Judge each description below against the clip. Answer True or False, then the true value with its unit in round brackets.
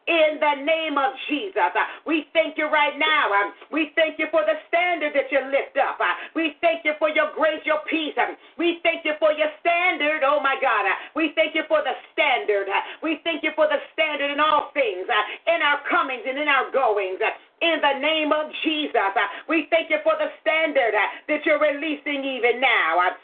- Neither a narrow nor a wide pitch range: False (1.9 semitones)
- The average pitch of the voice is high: True (305 Hz)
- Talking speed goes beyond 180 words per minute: True (195 wpm)